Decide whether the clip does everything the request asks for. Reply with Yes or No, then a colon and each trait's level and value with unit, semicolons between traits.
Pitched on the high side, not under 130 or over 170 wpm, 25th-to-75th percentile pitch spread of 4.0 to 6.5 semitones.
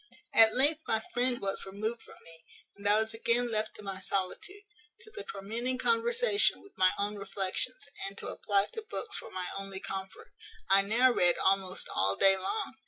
No: high, 210 Hz; average, 185 wpm; average, 4.7 semitones